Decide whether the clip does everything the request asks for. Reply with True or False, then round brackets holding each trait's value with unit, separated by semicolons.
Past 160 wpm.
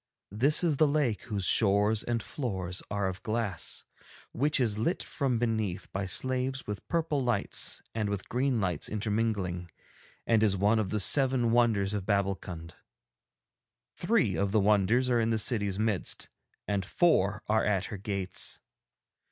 False (155 wpm)